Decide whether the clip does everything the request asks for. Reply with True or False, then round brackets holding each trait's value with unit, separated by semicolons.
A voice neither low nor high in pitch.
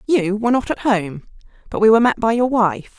False (215 Hz)